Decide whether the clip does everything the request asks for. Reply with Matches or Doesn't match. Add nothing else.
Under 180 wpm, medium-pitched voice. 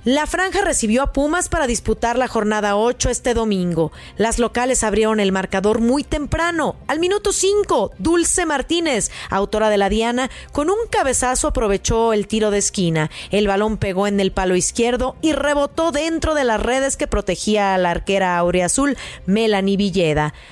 Doesn't match